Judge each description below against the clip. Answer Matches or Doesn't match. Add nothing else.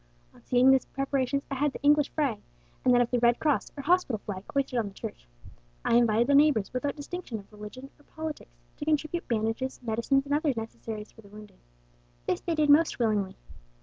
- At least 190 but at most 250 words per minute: Matches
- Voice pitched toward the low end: Doesn't match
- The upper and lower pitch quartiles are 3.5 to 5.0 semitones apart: Matches